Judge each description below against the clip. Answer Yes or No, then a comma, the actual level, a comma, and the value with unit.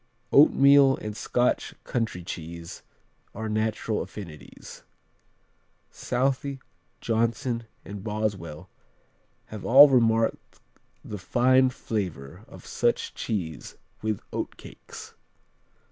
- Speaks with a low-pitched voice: Yes, low, 110 Hz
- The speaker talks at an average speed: No, slow, 85 wpm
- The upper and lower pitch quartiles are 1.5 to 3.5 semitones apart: No, average, 4.0 semitones